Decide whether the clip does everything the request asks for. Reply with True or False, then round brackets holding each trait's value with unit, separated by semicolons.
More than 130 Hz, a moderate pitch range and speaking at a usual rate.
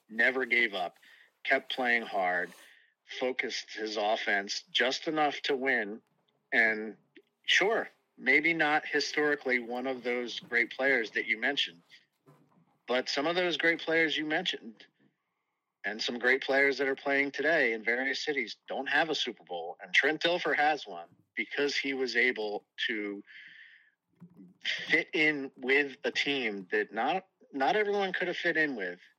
True (140 Hz; 3.7 semitones; 150 wpm)